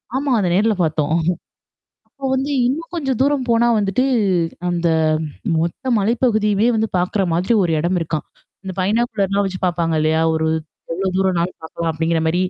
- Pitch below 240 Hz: Yes, high, 190 Hz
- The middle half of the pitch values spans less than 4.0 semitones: No, wide, 5.5 semitones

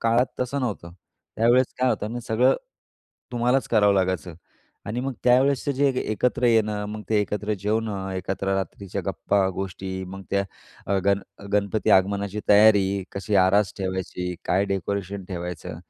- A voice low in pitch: Yes, low, 100 Hz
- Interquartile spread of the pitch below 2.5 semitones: No, average, 2.8 semitones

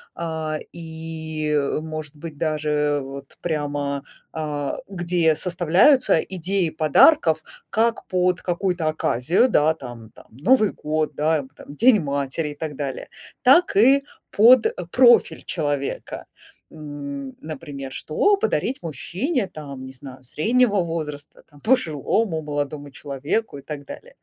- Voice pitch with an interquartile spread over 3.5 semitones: Yes, average, 3.9 semitones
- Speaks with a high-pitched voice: No, medium, 155 Hz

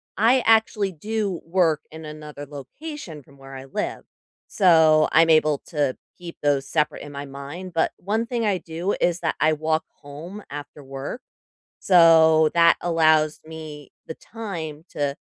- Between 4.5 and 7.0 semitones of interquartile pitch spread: No, average, 3.6 semitones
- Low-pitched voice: No, medium, 160 Hz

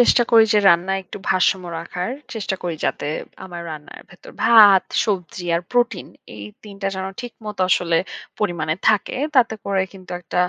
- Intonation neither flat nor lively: Yes, average, 3.5 semitones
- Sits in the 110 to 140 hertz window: No, high, 190 Hz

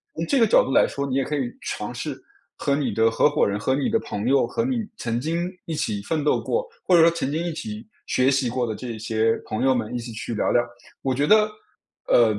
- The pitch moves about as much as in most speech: No, wide, 6.2 semitones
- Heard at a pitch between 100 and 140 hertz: Yes, low, 135 Hz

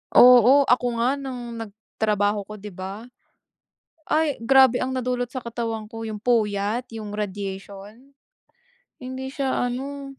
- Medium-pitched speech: No, high, 235 Hz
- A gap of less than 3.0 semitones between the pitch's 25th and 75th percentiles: No, average, 3.7 semitones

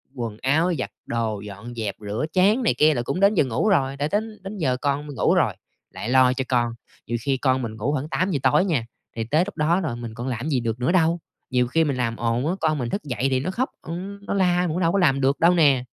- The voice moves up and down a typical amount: No, wide, 6.3 semitones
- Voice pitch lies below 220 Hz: Yes, medium, 140 Hz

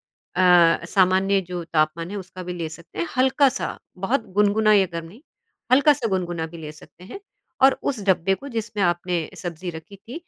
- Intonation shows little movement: No, average, 3.9 semitones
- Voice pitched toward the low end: No, medium, 185 Hz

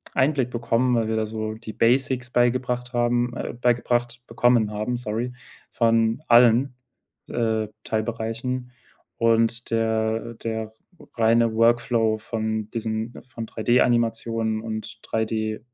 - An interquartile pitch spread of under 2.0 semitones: Yes, narrow, 1.5 semitones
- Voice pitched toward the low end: Yes, low, 115 Hz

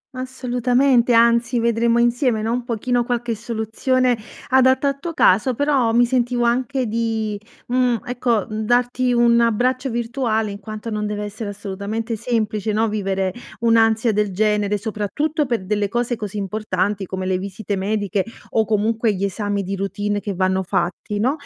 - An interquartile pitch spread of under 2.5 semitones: No, average, 2.8 semitones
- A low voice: No, high, 225 Hz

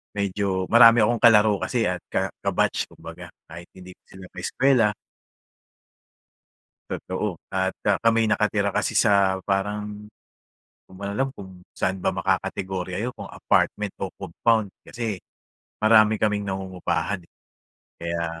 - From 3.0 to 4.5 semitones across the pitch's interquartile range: No, narrow, 2.4 semitones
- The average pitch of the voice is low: Yes, low, 100 Hz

